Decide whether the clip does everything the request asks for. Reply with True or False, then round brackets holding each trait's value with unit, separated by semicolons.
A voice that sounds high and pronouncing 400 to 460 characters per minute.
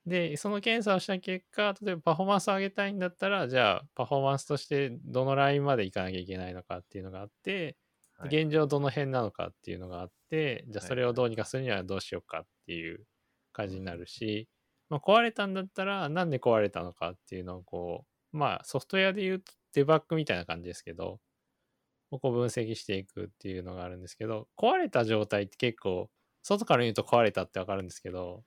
False (125 Hz; 455 characters per minute)